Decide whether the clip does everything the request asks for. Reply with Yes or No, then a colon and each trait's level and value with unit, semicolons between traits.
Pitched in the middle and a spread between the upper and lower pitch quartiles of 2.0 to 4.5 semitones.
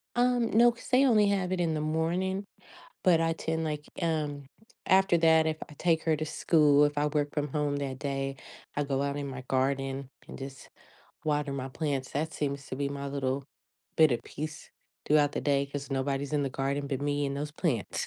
Yes: medium, 145 Hz; narrow, 2.6 semitones